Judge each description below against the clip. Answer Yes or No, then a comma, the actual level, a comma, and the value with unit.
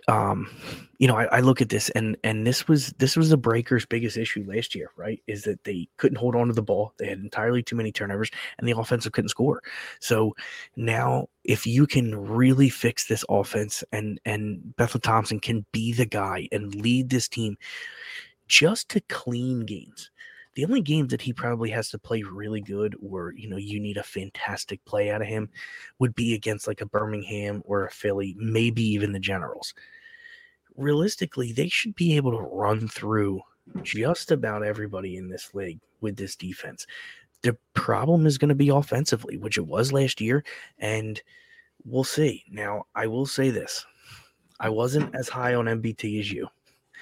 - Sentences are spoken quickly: No, average, 185 wpm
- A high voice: No, low, 115 Hz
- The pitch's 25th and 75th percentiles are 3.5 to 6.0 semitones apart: Yes, average, 3.9 semitones